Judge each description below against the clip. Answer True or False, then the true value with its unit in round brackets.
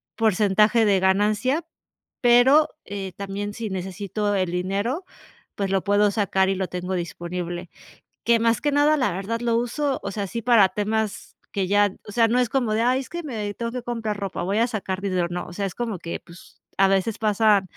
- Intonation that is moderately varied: True (3.3 semitones)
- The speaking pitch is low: False (205 Hz)